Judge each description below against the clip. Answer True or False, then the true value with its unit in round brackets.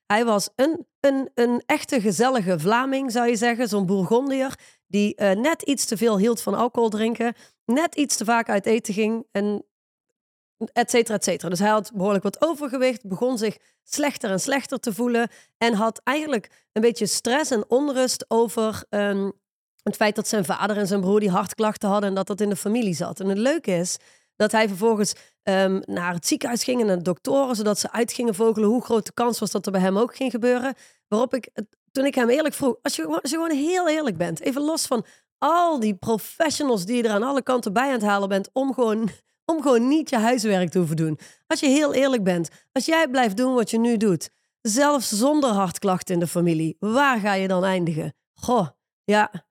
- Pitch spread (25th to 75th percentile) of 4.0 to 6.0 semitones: True (4.3 semitones)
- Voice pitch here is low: False (230 Hz)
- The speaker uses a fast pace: True (215 wpm)